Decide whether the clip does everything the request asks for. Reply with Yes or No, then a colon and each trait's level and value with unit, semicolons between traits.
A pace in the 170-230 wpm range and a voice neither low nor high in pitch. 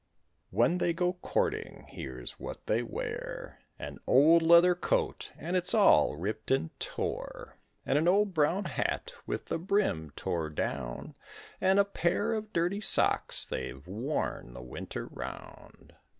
No: average, 145 wpm; medium, 165 Hz